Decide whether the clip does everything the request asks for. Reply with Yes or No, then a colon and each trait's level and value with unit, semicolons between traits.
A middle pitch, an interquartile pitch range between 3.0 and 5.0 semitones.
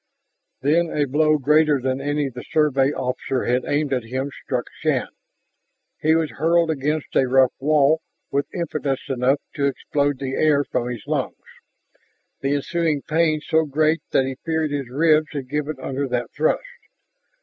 No: medium, 145 Hz; narrow, 2.6 semitones